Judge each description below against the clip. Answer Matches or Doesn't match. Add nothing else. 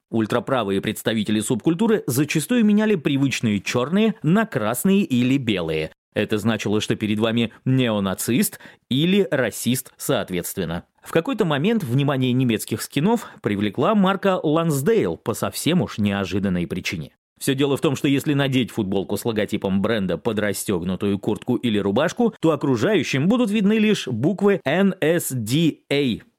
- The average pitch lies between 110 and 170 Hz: Matches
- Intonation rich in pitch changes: Matches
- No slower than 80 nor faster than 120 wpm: Doesn't match